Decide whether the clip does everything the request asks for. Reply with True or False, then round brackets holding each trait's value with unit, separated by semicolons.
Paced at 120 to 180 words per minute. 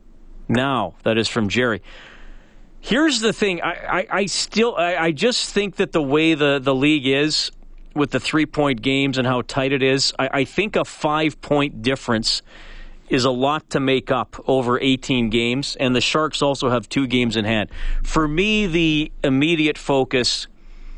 True (175 wpm)